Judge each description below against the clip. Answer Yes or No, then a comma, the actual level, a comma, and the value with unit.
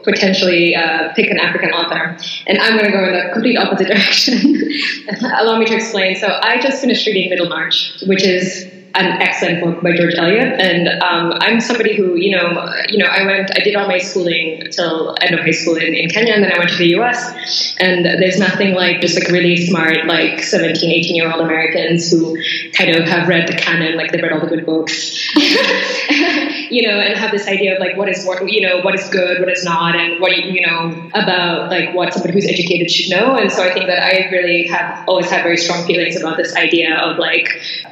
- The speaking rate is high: Yes, fast, 225 wpm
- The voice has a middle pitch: Yes, medium, 180 Hz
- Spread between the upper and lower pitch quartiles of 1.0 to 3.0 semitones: Yes, narrow, 2.6 semitones